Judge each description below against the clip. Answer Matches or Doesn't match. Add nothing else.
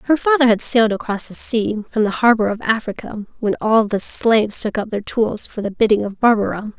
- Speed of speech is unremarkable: Doesn't match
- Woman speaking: Matches